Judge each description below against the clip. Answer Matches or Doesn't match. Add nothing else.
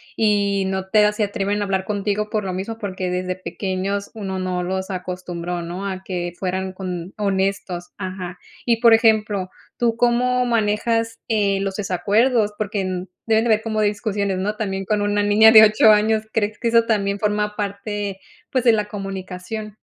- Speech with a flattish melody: Matches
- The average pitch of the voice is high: Matches